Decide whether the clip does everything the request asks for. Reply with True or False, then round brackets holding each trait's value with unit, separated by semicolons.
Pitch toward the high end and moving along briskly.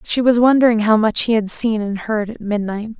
True (220 Hz; 240 wpm)